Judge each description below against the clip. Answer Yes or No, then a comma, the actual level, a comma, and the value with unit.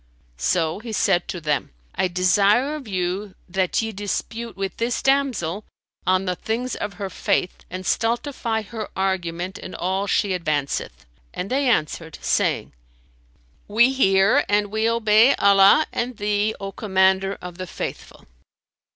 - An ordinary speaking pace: Yes, average, 145 wpm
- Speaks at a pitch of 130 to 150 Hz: No, high, 200 Hz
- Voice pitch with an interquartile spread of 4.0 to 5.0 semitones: No, average, 3.5 semitones